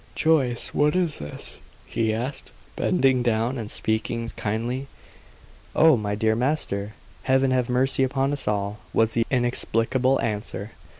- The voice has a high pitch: No, low, 120 Hz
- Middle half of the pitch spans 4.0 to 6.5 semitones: No, average, 3.3 semitones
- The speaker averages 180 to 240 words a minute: No, slow, 135 wpm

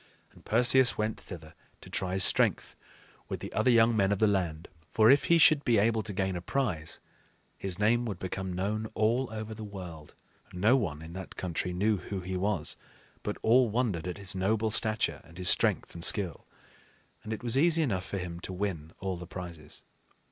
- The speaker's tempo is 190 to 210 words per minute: Yes, average, 200 wpm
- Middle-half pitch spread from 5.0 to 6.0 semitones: No, average, 3.7 semitones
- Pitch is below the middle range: Yes, low, 100 Hz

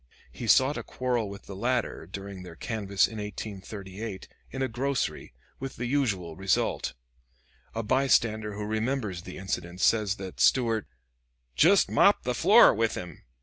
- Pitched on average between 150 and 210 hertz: No, low, 105 Hz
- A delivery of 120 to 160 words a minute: Yes, average, 150 wpm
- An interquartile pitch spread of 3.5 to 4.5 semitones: Yes, average, 3.9 semitones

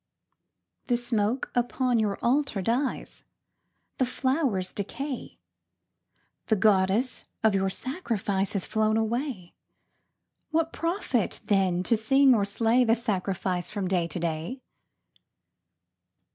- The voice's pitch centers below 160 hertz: No, high, 220 Hz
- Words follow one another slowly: Yes, slow, 115 wpm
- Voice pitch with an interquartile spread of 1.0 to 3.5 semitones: No, average, 4.9 semitones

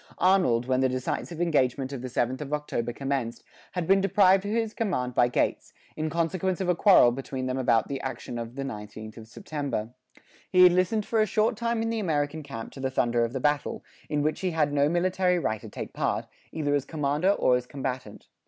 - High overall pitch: No, medium, 145 Hz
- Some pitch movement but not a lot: No, wide, 6.2 semitones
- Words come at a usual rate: No, fast, 220 wpm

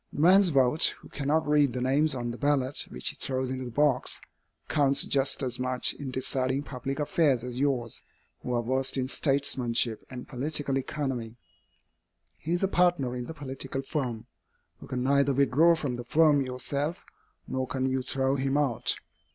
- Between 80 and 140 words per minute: No, average, 175 wpm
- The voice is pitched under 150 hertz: Yes, low, 135 Hz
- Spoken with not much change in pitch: Yes, narrow, 2.3 semitones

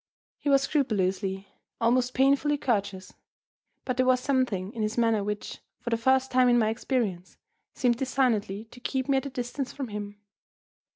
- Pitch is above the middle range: Yes, high, 240 Hz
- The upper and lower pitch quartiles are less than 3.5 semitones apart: No, average, 4.0 semitones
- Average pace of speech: Yes, average, 170 wpm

